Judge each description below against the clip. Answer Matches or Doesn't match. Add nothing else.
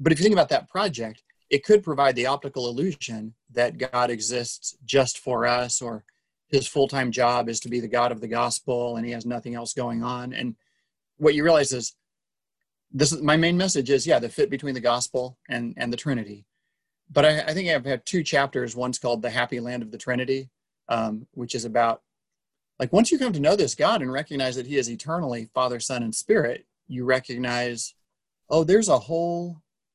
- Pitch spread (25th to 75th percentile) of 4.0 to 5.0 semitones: Doesn't match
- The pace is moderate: Doesn't match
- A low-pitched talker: Matches